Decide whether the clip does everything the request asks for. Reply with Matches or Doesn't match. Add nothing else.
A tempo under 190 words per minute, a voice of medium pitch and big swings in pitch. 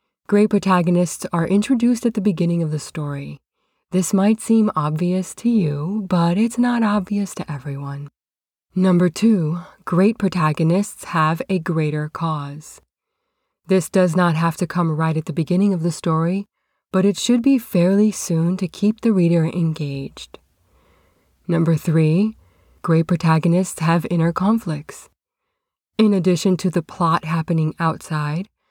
Doesn't match